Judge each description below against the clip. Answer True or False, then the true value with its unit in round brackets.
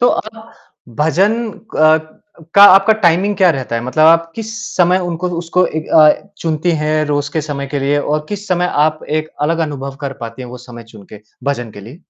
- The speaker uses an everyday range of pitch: True (4.4 semitones)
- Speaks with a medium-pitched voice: True (155 Hz)